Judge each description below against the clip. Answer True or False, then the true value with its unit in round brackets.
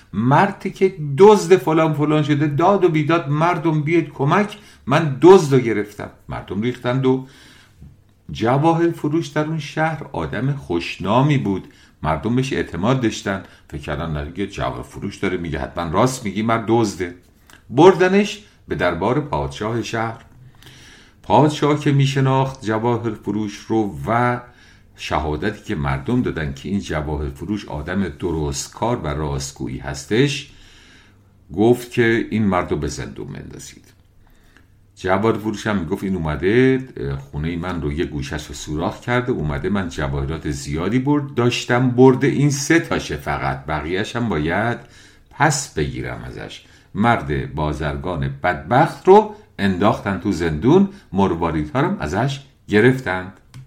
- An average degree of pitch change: False (8.5 semitones)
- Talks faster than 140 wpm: False (135 wpm)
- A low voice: True (110 Hz)